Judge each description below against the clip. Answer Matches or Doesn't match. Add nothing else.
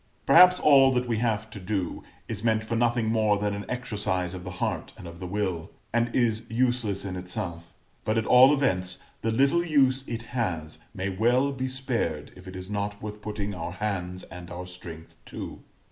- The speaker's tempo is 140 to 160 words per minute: Doesn't match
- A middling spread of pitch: Matches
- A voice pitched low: Matches